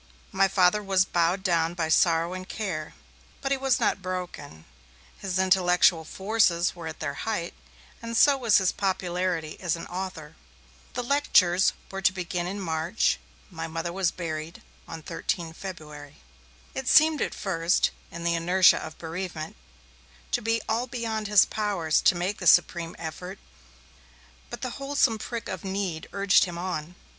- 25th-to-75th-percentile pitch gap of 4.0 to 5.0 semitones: No, average, 3.3 semitones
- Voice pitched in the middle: Yes, medium, 180 Hz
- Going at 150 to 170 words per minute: Yes, average, 160 wpm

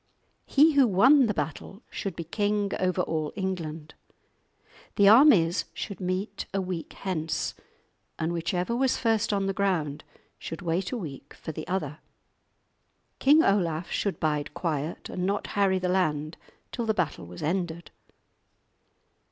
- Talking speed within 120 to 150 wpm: Yes, average, 145 wpm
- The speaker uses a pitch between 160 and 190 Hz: Yes, medium, 185 Hz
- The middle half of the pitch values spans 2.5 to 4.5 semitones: Yes, average, 3.9 semitones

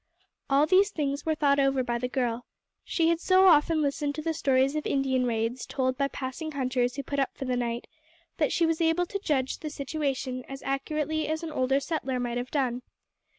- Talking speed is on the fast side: Yes, fast, 210 wpm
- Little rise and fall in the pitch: No, average, 3.4 semitones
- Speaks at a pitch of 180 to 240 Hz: No, very high, 275 Hz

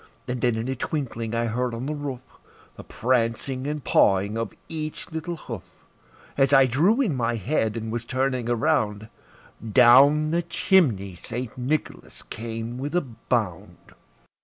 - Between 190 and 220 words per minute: No, average, 155 wpm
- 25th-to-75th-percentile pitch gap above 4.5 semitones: No, average, 4.2 semitones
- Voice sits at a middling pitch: No, low, 125 Hz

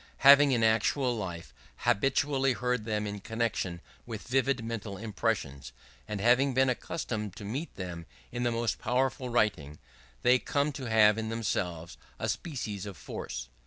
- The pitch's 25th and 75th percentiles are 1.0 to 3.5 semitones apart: No, average, 4.0 semitones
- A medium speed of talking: Yes, average, 160 wpm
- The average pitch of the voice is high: No, low, 115 Hz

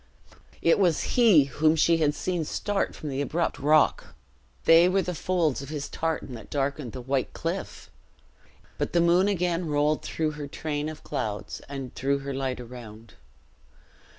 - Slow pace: No, average, 165 wpm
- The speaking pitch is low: No, medium, 150 Hz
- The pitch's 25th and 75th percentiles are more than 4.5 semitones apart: No, average, 3.6 semitones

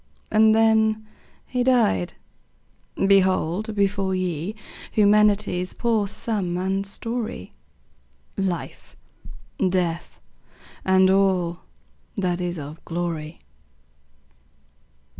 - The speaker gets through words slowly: Yes, slow, 80 wpm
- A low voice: No, high, 190 Hz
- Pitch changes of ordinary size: Yes, average, 3.3 semitones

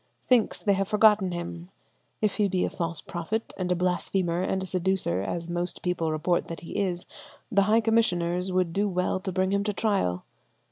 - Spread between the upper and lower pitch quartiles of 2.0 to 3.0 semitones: Yes, narrow, 2.5 semitones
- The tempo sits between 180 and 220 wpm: Yes, average, 195 wpm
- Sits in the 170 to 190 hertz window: Yes, medium, 185 Hz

